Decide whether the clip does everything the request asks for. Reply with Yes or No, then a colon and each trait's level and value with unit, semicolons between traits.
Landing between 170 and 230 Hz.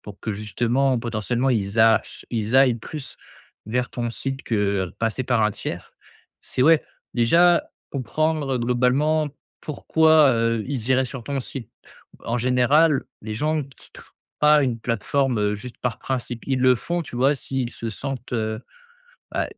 No: low, 125 Hz